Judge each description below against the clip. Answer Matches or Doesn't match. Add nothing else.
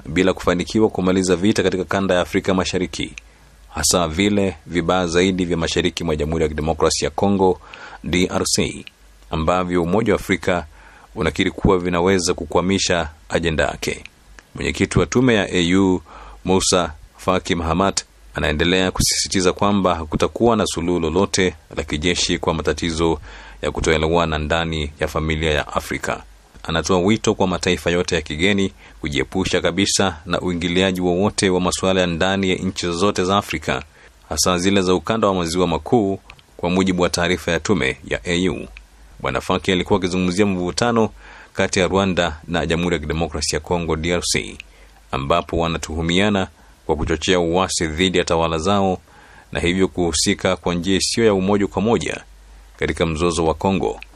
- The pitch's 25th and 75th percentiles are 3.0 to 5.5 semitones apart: Doesn't match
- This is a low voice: Matches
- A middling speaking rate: Doesn't match